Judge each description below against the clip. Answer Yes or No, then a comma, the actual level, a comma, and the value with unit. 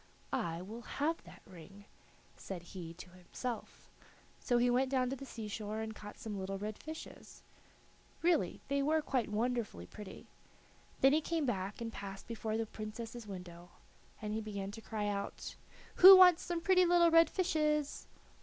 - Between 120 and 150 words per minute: No, average, 165 wpm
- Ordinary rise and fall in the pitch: No, wide, 6.0 semitones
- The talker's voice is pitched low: No, high, 225 Hz